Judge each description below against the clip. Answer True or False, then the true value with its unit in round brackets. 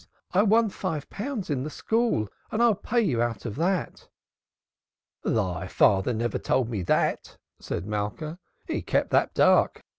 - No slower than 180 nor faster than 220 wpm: False (155 wpm)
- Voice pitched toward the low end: False (150 Hz)